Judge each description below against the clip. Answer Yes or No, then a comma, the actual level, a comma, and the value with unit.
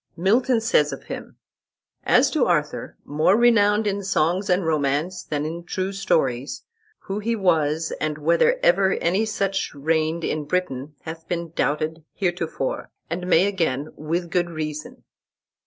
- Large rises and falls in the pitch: No, average, 3.9 semitones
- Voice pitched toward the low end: No, medium, 170 Hz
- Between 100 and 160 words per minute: Yes, average, 145 wpm